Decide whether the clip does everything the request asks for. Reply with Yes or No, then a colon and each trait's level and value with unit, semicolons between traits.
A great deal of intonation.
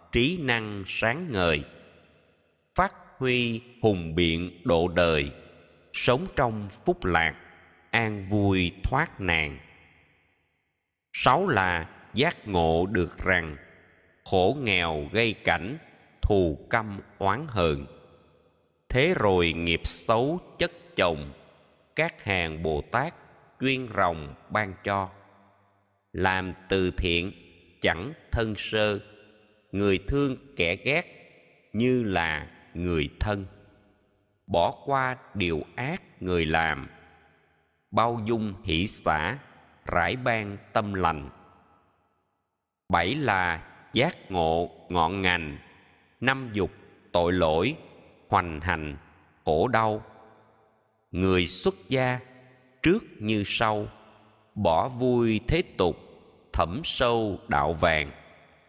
No: average, 4.8 semitones